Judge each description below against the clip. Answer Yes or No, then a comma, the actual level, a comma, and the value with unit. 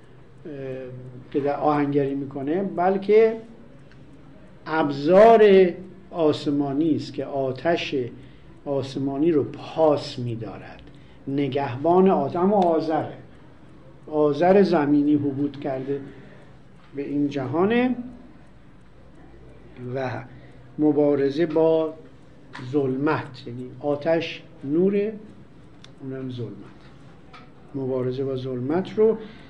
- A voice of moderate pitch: Yes, medium, 145 Hz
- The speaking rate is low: Yes, slow, 75 wpm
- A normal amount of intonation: Yes, average, 3.6 semitones